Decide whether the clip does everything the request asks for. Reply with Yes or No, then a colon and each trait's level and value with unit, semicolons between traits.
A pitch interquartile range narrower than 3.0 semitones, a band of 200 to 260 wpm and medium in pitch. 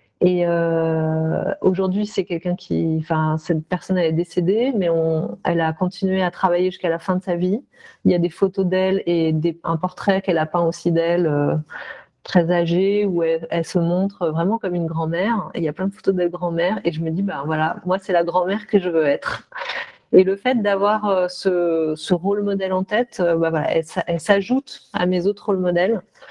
Yes: narrow, 2.5 semitones; average, 210 wpm; medium, 180 Hz